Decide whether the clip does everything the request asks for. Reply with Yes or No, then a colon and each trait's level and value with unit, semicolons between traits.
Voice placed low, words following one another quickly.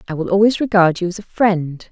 No: high, 190 Hz; fast, 250 wpm